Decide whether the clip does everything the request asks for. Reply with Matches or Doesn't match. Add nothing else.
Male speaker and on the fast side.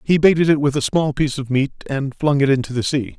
Matches